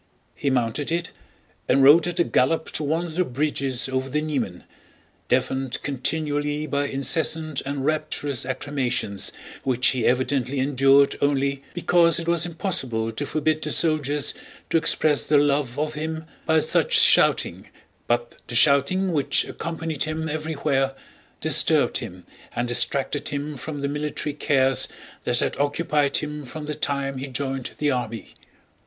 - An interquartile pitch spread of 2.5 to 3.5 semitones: Yes, average, 2.8 semitones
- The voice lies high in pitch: No, medium, 145 Hz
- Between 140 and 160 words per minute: Yes, average, 150 wpm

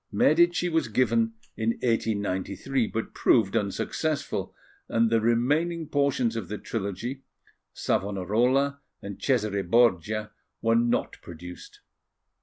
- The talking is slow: Yes, slow, 105 wpm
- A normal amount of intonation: Yes, average, 4.8 semitones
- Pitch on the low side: Yes, low, 115 Hz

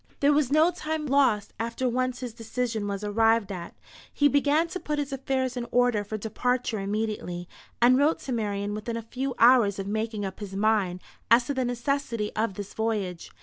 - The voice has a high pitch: Yes, high, 230 Hz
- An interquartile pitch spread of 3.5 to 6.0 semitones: Yes, average, 3.9 semitones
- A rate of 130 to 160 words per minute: No, average, 190 wpm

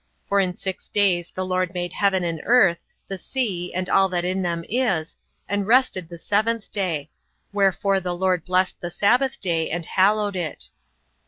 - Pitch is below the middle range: No, medium, 185 Hz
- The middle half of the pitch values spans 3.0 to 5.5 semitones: No, narrow, 2.5 semitones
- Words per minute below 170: No, average, 175 wpm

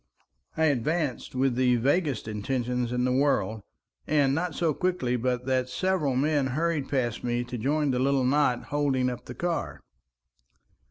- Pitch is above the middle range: No, low, 130 Hz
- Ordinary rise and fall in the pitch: Yes, average, 3.1 semitones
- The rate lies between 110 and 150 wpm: No, average, 160 wpm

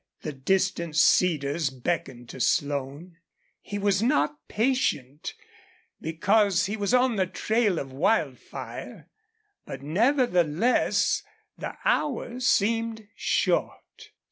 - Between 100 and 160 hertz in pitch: No, medium, 185 Hz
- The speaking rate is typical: No, slow, 100 wpm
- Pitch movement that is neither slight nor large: No, wide, 7.2 semitones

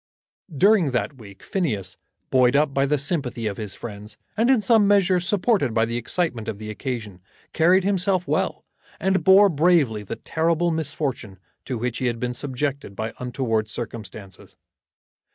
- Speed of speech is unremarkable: Yes, average, 160 wpm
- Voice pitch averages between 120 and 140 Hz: Yes, low, 135 Hz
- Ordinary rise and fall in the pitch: No, wide, 7.8 semitones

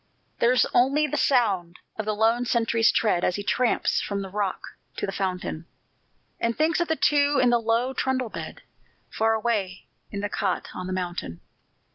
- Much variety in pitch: No, average, 4.3 semitones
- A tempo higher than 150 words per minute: Yes, average, 180 wpm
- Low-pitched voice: No, high, 225 Hz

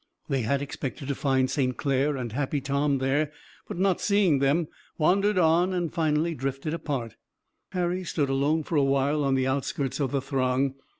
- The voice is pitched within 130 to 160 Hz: Yes, medium, 140 Hz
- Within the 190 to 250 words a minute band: No, average, 180 wpm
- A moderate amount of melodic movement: Yes, average, 3.1 semitones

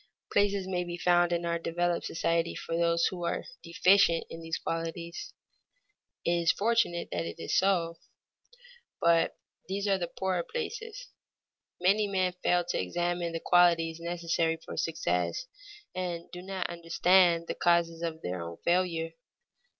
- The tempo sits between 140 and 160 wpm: Yes, average, 150 wpm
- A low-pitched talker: No, medium, 170 Hz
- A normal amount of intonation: No, narrow, 1.7 semitones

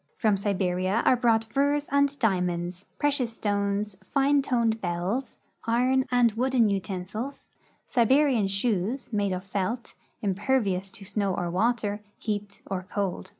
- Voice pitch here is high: Yes, high, 210 Hz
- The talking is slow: Yes, slow, 130 wpm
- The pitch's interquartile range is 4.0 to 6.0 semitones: Yes, average, 4.3 semitones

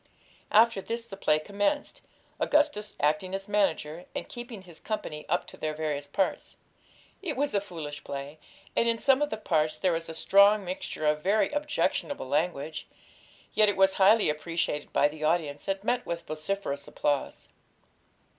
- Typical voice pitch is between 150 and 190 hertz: Yes, medium, 185 Hz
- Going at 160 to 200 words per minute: Yes, average, 165 wpm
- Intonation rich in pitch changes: Yes, wide, 5.7 semitones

